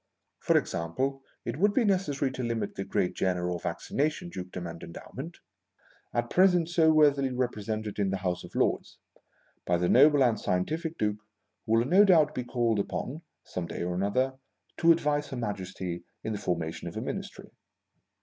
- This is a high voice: No, low, 120 Hz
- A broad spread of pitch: Yes, wide, 8.0 semitones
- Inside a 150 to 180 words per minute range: Yes, average, 175 wpm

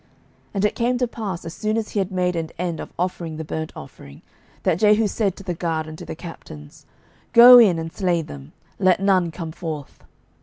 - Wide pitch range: No, average, 4.3 semitones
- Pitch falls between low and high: Yes, medium, 180 Hz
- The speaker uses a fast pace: Yes, fast, 220 wpm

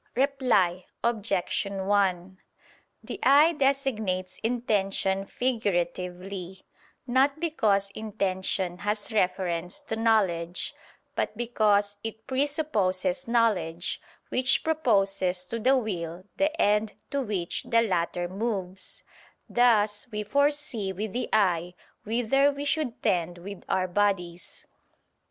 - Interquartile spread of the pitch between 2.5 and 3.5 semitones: No, average, 4.7 semitones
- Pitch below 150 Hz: No, high, 205 Hz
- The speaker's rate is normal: No, slow, 105 wpm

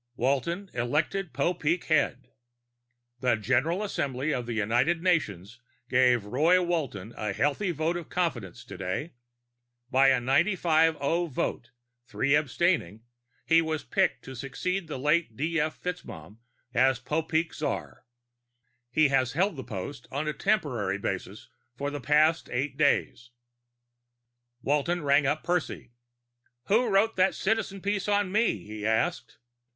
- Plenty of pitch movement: Yes, wide, 5.8 semitones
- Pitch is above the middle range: No, medium, 150 Hz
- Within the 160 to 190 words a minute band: No, slow, 135 wpm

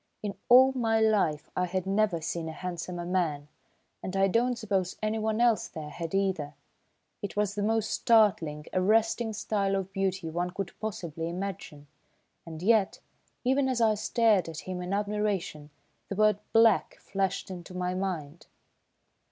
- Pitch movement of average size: Yes, average, 3.7 semitones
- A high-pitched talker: Yes, high, 195 Hz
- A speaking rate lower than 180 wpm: Yes, average, 155 wpm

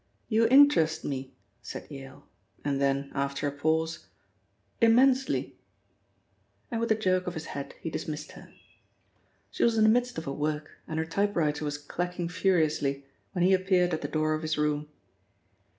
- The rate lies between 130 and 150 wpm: No, average, 165 wpm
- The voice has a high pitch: No, medium, 160 Hz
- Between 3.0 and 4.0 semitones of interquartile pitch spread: No, average, 4.5 semitones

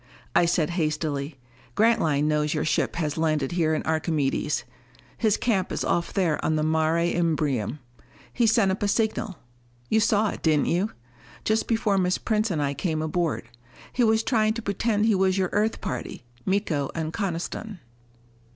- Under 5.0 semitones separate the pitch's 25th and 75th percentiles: No, average, 5.3 semitones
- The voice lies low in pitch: No, medium, 175 Hz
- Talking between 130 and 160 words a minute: No, average, 170 wpm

